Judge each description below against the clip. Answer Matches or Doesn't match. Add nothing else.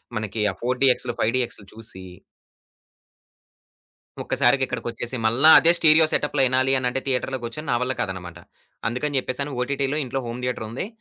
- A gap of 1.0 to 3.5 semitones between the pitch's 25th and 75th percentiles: Matches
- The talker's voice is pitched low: Matches